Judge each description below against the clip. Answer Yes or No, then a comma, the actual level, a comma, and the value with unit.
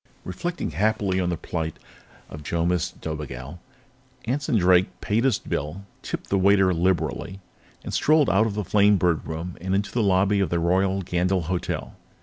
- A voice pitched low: Yes, very low, 95 Hz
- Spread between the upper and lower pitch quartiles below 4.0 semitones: Yes, average, 2.9 semitones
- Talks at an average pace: Yes, average, 160 wpm